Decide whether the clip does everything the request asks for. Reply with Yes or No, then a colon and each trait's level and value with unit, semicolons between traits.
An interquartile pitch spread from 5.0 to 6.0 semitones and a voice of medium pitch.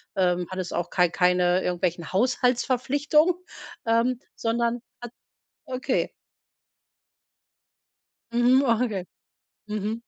No: wide, 5.5 semitones; high, 230 Hz